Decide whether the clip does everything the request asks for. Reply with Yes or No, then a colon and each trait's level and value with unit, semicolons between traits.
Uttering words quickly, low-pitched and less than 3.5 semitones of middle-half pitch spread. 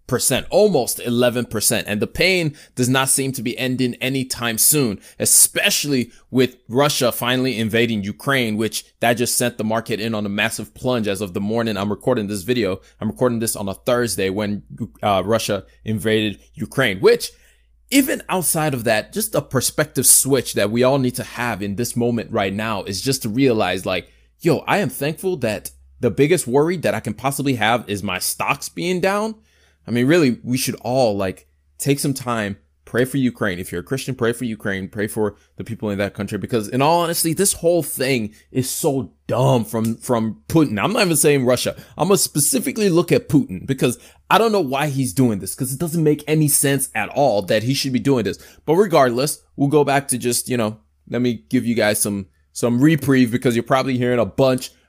No: fast, 210 wpm; low, 120 Hz; average, 4.4 semitones